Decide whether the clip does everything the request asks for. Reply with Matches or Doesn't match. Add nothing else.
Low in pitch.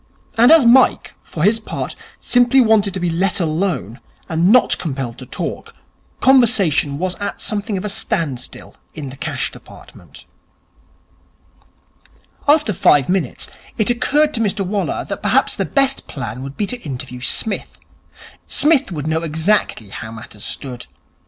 Doesn't match